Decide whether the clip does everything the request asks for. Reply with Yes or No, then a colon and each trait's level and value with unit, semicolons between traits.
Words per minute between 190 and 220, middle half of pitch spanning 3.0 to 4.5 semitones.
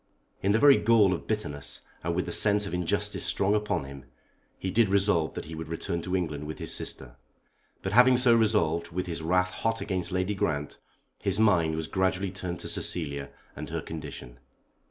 Yes: average, 195 wpm; average, 4.2 semitones